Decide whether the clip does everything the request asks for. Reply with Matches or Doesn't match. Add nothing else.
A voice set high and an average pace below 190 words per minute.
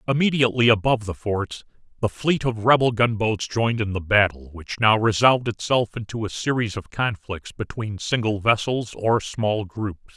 Doesn't match